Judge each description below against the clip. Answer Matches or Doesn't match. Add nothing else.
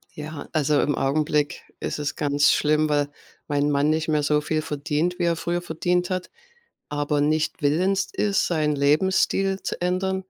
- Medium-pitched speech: Matches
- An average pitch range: Matches